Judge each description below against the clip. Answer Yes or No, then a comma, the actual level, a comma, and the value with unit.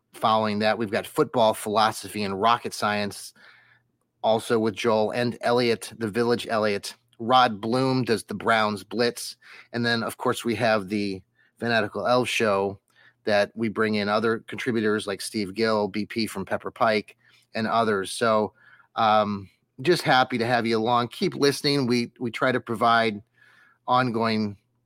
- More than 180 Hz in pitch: No, low, 115 Hz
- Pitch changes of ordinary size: No, narrow, 2.2 semitones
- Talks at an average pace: Yes, average, 155 wpm